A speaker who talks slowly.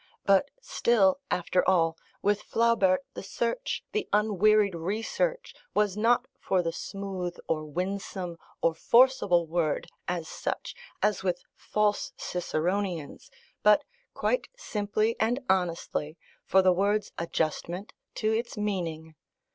Yes: slow, 120 wpm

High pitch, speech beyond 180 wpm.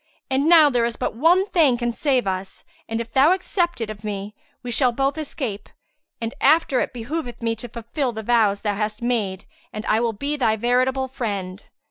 Yes: high, 240 Hz; average, 200 wpm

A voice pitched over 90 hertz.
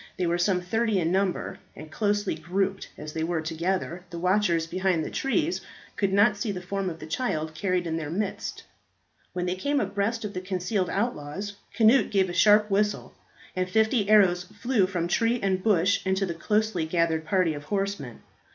Yes: high, 190 Hz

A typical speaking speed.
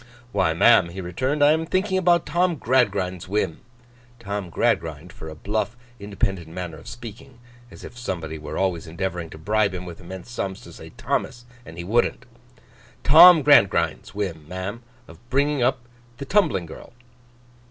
Yes: average, 160 wpm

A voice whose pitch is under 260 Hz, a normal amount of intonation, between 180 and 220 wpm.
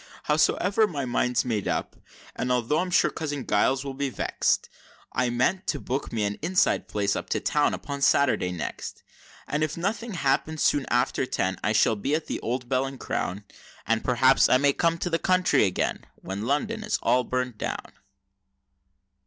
Yes: low, 135 Hz; average, 4.6 semitones; average, 185 wpm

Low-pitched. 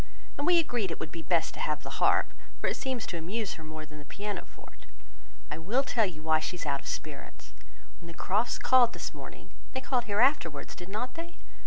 No: high, 190 Hz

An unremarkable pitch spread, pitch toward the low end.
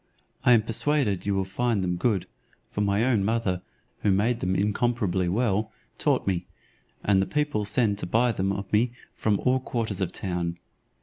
Yes: average, 3.5 semitones; low, 105 Hz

